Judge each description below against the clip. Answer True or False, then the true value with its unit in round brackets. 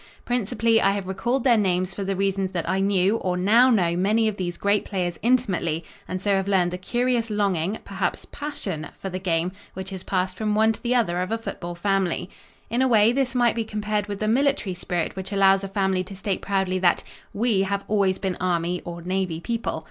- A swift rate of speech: True (215 wpm)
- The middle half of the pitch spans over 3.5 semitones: False (3.0 semitones)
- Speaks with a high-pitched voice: True (195 Hz)